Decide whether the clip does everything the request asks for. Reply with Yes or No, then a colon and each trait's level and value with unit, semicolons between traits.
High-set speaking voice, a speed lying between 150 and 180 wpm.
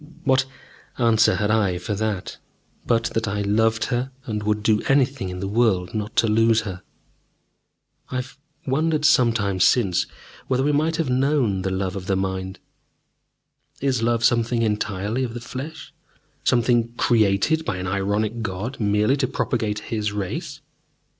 No: low, 110 Hz; average, 155 wpm